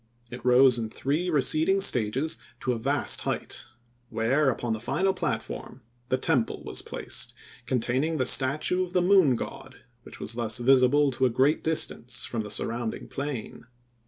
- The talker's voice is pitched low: Yes, low, 130 Hz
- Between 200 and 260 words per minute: No, average, 160 wpm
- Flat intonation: No, average, 4.2 semitones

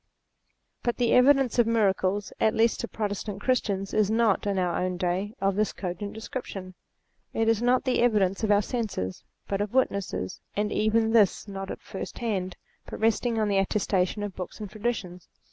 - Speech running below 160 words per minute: No, average, 180 wpm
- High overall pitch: Yes, high, 205 Hz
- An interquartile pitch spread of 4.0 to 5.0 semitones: No, average, 2.8 semitones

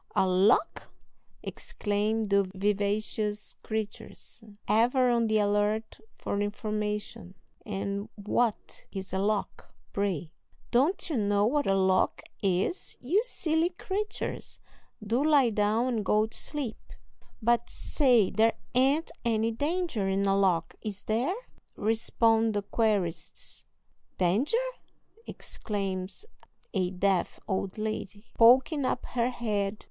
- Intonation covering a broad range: No, average, 3.2 semitones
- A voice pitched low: No, high, 215 Hz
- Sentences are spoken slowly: Yes, slow, 120 wpm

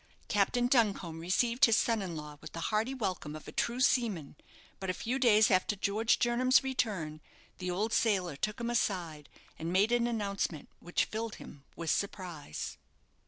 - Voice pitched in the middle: No, high, 205 Hz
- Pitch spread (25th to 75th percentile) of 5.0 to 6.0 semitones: Yes, wide, 5.4 semitones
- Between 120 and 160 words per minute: No, average, 170 wpm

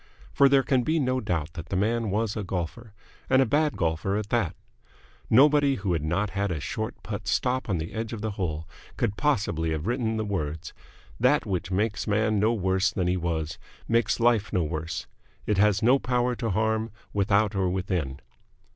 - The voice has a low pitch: Yes, low, 105 Hz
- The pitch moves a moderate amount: Yes, average, 4.5 semitones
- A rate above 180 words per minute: Yes, average, 200 wpm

